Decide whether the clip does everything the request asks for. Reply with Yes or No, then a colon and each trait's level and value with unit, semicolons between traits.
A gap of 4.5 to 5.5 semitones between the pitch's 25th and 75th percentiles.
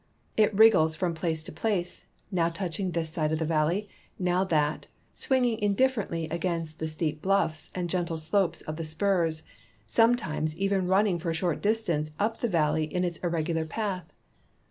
No: average, 3.8 semitones